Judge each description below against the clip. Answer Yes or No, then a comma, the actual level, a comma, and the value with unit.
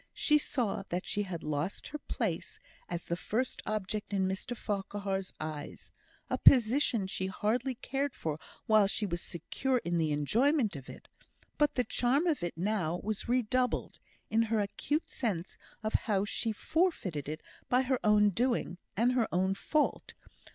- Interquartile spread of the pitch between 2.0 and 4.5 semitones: No, wide, 5.5 semitones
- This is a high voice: Yes, high, 210 Hz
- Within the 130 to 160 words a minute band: No, average, 170 wpm